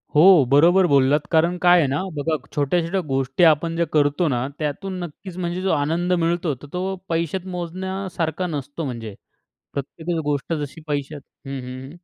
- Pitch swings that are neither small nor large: Yes, average, 3.6 semitones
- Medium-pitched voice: Yes, medium, 160 Hz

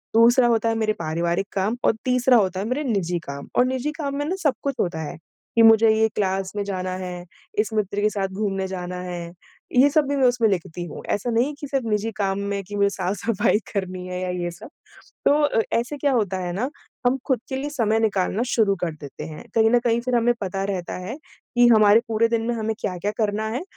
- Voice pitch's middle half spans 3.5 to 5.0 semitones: Yes, average, 4.2 semitones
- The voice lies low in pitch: No, high, 215 Hz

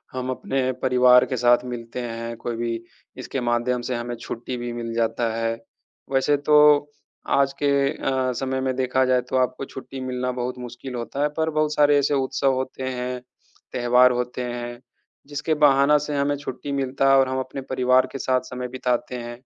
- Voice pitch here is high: No, low, 125 Hz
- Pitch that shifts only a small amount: Yes, narrow, 1.8 semitones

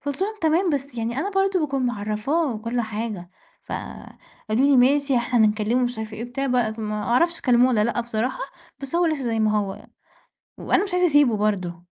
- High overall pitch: Yes, high, 245 Hz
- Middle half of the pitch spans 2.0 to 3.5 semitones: No, average, 4.8 semitones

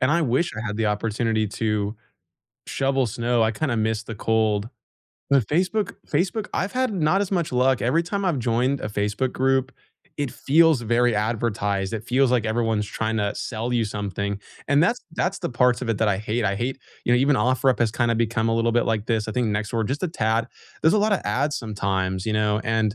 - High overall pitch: No, low, 115 Hz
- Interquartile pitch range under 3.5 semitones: No, average, 3.9 semitones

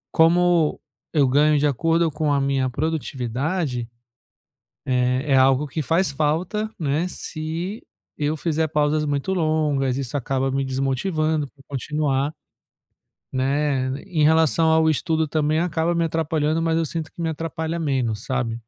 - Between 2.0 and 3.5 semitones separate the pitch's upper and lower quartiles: Yes, average, 3.0 semitones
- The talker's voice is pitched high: No, medium, 150 Hz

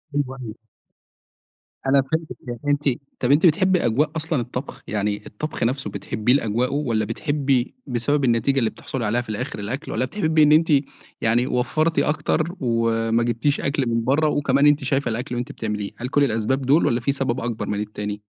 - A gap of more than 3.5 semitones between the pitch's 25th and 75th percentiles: Yes, average, 4.0 semitones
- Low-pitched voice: Yes, low, 125 Hz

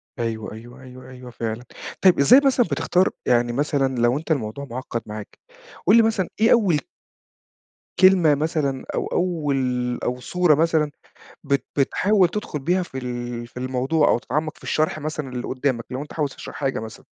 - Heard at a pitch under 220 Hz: Yes, medium, 140 Hz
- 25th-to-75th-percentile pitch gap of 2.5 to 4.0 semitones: No, average, 4.8 semitones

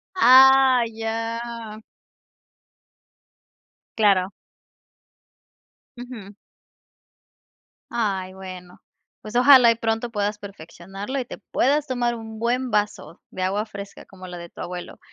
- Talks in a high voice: Yes, high, 220 Hz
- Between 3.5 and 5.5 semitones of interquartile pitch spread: Yes, average, 3.8 semitones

